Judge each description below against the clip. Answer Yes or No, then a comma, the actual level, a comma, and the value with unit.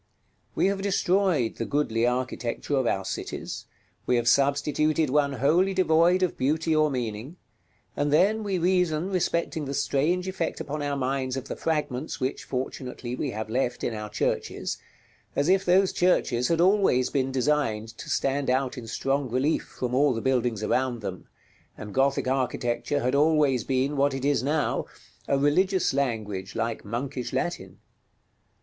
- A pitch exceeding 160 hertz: No, medium, 140 Hz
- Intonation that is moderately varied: Yes, average, 4.1 semitones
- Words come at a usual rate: Yes, average, 160 wpm